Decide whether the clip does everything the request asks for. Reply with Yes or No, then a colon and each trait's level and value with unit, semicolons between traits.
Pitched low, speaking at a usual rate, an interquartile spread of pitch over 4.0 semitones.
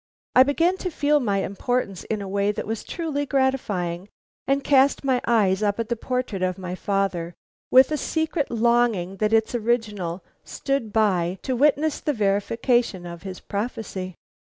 No: high, 225 Hz; average, 165 wpm; average, 5.3 semitones